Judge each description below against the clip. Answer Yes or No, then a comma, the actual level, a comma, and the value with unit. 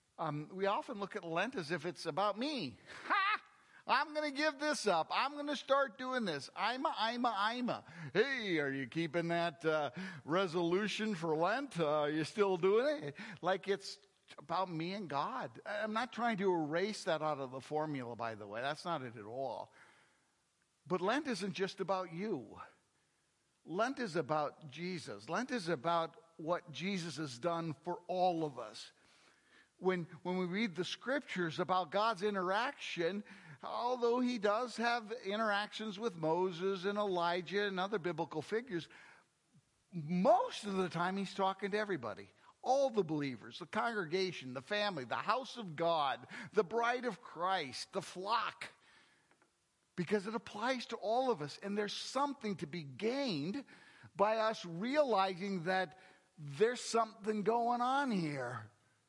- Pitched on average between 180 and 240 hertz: Yes, high, 190 Hz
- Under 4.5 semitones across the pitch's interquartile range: No, average, 4.8 semitones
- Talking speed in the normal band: Yes, average, 160 wpm